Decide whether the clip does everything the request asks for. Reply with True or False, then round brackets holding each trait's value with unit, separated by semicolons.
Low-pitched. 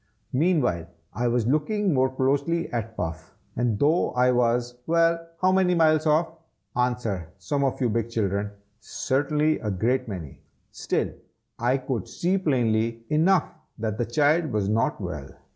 True (125 Hz)